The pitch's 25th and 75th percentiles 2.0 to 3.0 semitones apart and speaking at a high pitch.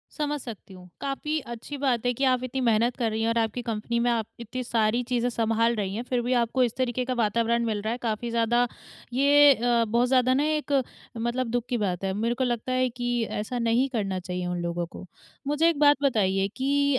Yes: narrow, 2.4 semitones; high, 240 Hz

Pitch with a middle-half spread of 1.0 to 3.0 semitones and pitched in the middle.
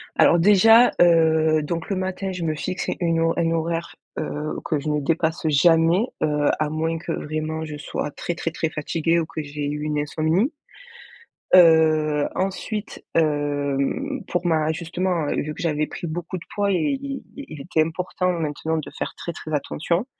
Yes: narrow, 2.4 semitones; medium, 160 Hz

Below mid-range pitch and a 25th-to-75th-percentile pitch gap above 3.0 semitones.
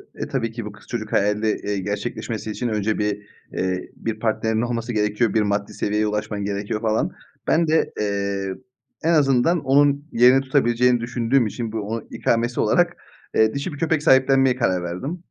Yes: low, 115 Hz; average, 3.5 semitones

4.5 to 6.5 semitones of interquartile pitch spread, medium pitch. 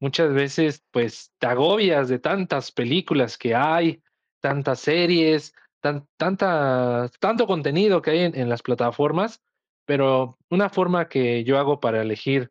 Yes: average, 4.9 semitones; medium, 145 Hz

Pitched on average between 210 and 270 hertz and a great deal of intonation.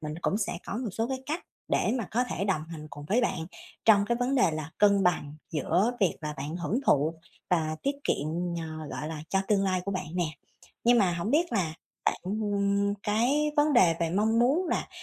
No: high, 200 Hz; wide, 6.3 semitones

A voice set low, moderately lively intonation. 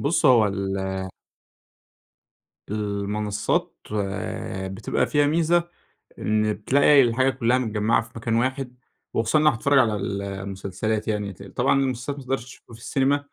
Yes: low, 115 Hz; average, 4.4 semitones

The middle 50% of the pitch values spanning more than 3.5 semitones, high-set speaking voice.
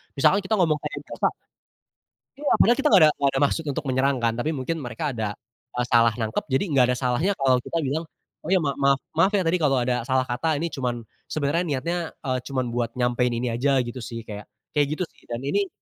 No: average, 4.8 semitones; low, 135 Hz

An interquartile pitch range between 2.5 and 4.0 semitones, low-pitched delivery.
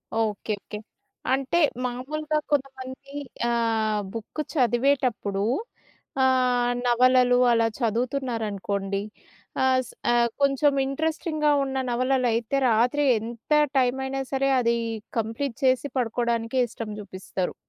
No: average, 2.8 semitones; high, 245 Hz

